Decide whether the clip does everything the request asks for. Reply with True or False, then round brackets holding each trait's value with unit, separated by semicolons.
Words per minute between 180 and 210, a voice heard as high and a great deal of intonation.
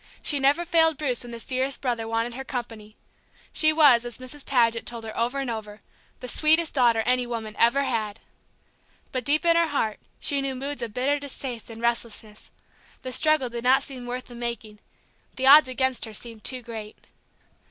False (190 wpm; 250 Hz; 3.1 semitones)